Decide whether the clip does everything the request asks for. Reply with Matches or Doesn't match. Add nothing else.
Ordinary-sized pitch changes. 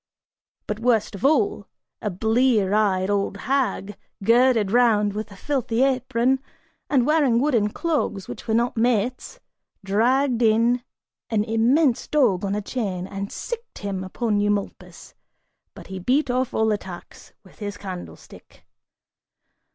Matches